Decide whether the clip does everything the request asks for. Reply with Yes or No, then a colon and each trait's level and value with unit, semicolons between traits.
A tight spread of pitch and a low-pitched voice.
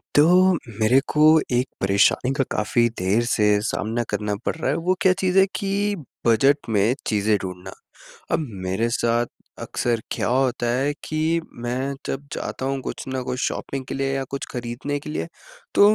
No: average, 3.9 semitones; low, 130 Hz